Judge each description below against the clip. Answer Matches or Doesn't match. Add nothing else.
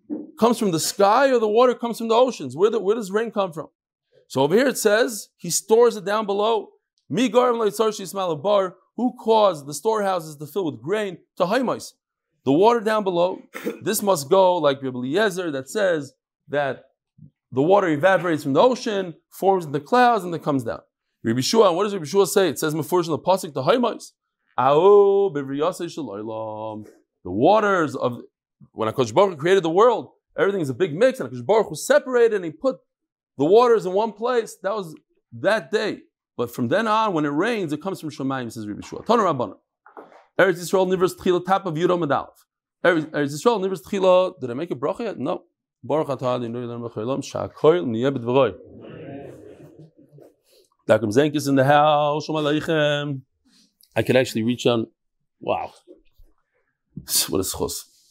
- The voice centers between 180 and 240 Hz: Matches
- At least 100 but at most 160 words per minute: Doesn't match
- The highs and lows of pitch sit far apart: Matches